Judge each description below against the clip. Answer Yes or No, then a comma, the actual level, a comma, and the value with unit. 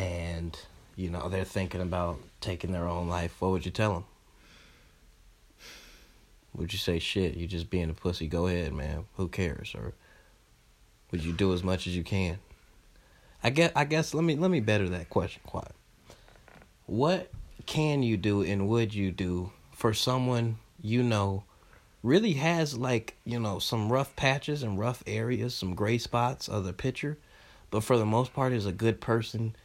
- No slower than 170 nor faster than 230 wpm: Yes, average, 180 wpm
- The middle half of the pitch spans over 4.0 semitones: Yes, average, 5.0 semitones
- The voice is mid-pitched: No, low, 100 Hz